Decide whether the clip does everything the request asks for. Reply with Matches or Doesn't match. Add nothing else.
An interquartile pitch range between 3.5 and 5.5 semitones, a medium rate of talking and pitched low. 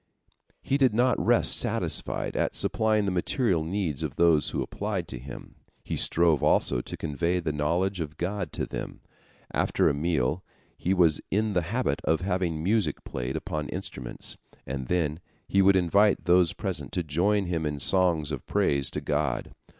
Matches